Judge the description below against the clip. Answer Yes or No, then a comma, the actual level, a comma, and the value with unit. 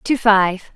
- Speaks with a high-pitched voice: Yes, high, 210 Hz